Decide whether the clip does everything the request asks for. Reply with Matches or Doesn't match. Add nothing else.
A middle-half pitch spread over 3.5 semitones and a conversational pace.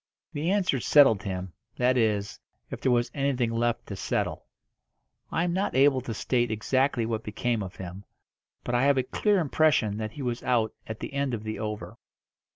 Matches